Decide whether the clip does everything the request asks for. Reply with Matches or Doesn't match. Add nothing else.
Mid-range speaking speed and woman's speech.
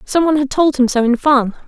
Doesn't match